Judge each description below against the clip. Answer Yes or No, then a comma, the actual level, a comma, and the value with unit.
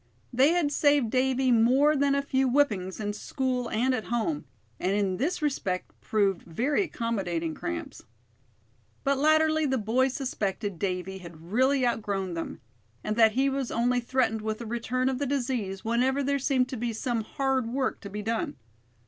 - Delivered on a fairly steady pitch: No, average, 4.4 semitones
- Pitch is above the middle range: Yes, high, 245 Hz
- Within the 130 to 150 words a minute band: No, average, 175 wpm